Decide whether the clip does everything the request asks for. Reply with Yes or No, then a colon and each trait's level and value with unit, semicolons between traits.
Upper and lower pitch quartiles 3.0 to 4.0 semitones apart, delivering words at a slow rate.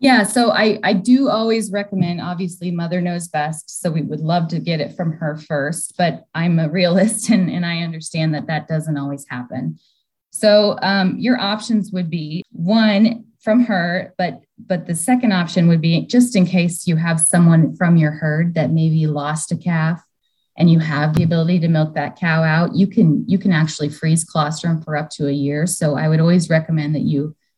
No: average, 3.4 semitones; average, 200 wpm